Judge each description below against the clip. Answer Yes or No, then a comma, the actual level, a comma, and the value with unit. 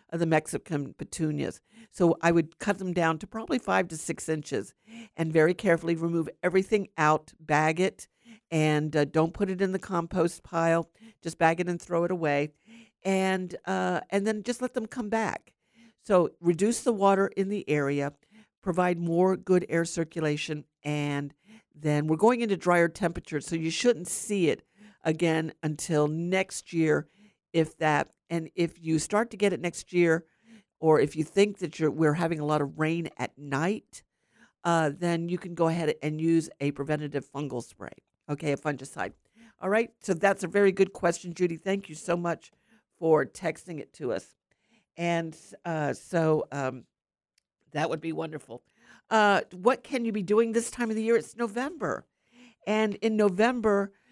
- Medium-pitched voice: Yes, medium, 170 Hz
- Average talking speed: Yes, average, 175 wpm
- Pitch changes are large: No, average, 4.5 semitones